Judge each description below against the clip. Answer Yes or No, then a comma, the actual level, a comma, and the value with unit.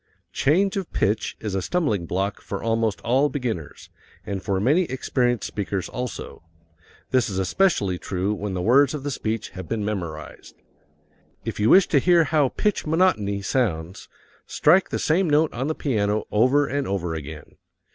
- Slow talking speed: No, average, 165 wpm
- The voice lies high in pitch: No, low, 115 Hz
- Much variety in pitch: Yes, wide, 6.8 semitones